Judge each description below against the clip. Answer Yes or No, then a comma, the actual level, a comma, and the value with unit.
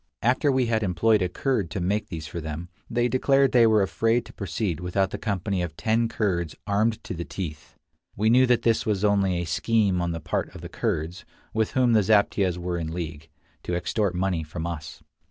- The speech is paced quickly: Yes, fast, 210 wpm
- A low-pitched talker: Yes, very low, 95 Hz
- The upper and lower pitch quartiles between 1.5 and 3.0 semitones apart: No, average, 4.5 semitones